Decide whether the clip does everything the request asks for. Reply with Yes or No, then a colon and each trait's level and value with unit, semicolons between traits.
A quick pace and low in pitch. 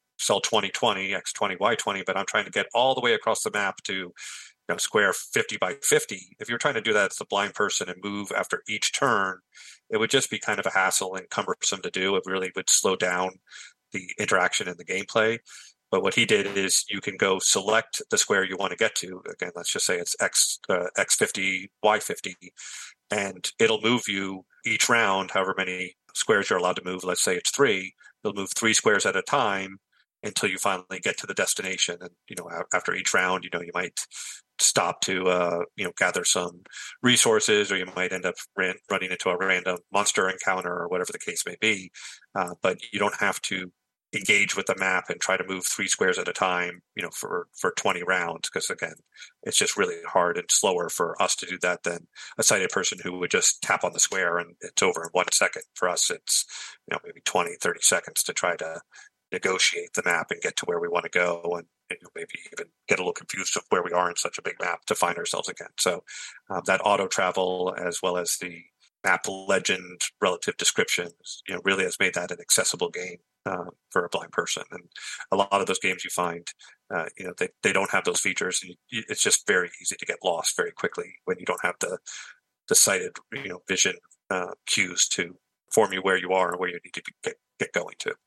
Yes: fast, 230 wpm; low, 110 Hz